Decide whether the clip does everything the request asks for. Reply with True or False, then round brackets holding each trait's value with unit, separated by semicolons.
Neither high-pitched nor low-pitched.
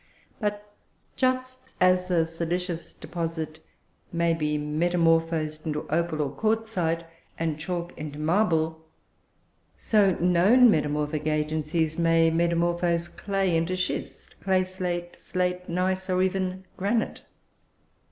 True (170 Hz)